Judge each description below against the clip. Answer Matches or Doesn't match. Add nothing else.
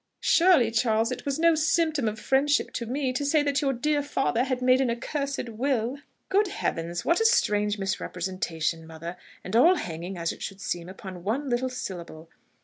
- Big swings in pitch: Matches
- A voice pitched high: Matches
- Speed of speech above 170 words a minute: Matches